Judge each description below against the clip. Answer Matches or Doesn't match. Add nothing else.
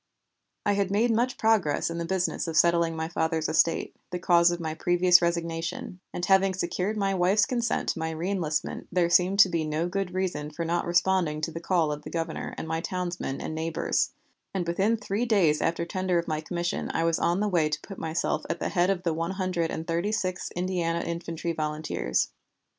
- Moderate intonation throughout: Doesn't match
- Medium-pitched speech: Matches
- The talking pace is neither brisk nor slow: Doesn't match